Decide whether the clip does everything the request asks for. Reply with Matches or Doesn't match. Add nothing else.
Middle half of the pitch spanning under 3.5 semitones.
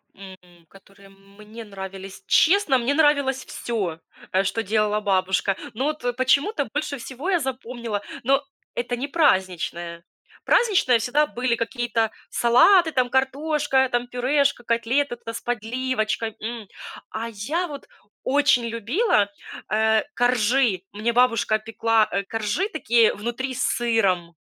Doesn't match